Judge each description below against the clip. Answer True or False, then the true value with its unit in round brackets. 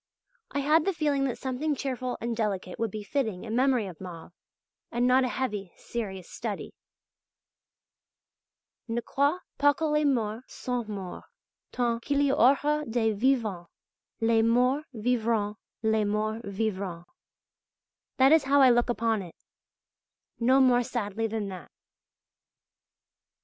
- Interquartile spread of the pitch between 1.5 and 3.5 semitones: False (4.0 semitones)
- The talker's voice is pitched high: True (235 Hz)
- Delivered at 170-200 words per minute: False (140 wpm)